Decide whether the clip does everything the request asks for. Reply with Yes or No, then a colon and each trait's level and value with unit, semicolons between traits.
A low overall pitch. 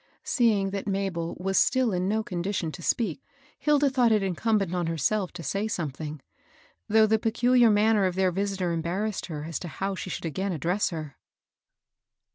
No: high, 195 Hz